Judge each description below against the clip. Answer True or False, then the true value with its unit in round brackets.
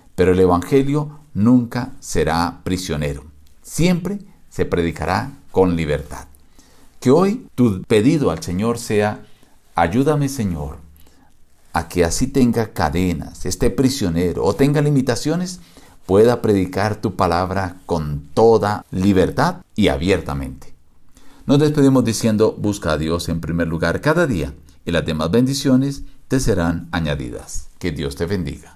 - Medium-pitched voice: False (95 Hz)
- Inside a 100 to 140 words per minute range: True (125 wpm)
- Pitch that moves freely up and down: True (7.3 semitones)